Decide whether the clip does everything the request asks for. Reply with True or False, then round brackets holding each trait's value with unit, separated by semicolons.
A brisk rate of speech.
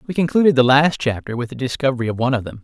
True (275 wpm)